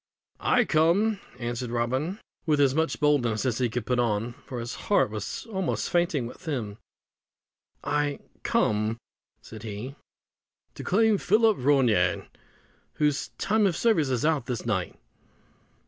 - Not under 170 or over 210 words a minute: No, average, 140 wpm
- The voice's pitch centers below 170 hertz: Yes, low, 135 Hz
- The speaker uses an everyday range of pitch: No, wide, 6.1 semitones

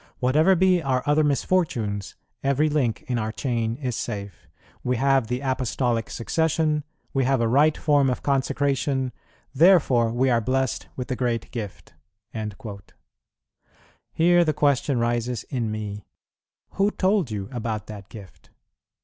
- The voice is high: No, low, 130 Hz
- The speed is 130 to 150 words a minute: Yes, average, 140 wpm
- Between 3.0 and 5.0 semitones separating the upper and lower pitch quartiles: Yes, average, 4.1 semitones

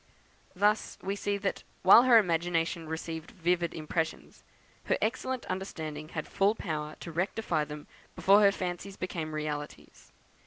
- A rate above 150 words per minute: No, average, 140 wpm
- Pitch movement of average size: Yes, average, 4.0 semitones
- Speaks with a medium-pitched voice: Yes, medium, 175 Hz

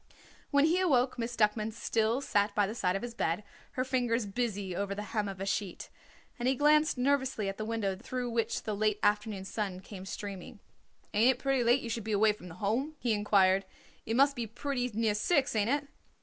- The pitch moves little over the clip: No, average, 3.6 semitones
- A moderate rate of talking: No, fast, 215 wpm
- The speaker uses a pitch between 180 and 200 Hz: No, high, 220 Hz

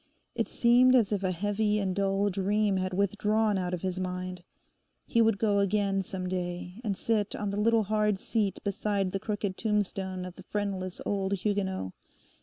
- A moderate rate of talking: Yes, average, 180 wpm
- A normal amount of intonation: No, narrow, 2.1 semitones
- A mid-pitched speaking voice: No, high, 200 Hz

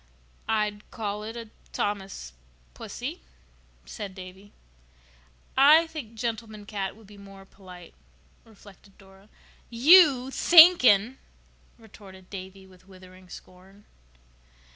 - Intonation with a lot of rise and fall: No, average, 3.1 semitones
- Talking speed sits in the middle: No, slow, 100 wpm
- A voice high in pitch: Yes, high, 205 Hz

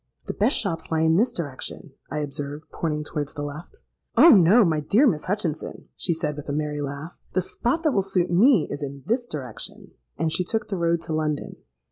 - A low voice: No, medium, 160 Hz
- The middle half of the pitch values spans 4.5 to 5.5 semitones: Yes, average, 4.8 semitones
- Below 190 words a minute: No, average, 200 wpm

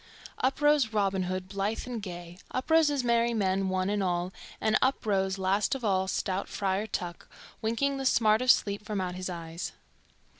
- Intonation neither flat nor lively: Yes, average, 3.9 semitones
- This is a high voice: Yes, high, 200 Hz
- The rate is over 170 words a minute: Yes, average, 190 wpm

